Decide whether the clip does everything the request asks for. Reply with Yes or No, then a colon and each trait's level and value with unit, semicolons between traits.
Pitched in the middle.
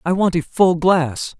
Yes: medium, 170 Hz